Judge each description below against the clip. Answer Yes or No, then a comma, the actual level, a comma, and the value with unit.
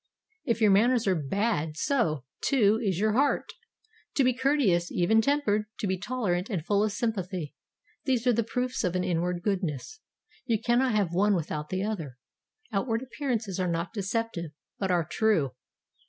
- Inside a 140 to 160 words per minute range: No, average, 170 wpm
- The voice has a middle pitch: No, high, 205 Hz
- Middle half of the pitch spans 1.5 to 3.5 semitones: No, average, 4.8 semitones